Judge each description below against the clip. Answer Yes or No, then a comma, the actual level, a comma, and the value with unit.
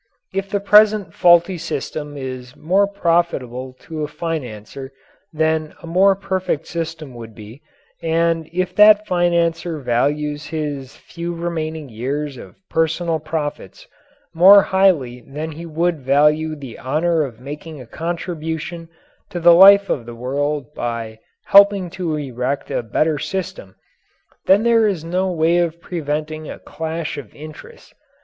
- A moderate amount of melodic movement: Yes, average, 3.3 semitones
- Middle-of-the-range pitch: Yes, medium, 160 Hz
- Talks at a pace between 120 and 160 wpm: Yes, average, 140 wpm